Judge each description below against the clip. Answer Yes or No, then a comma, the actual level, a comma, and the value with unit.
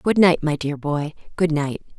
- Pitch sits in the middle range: Yes, medium, 155 Hz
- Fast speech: Yes, fast, 210 wpm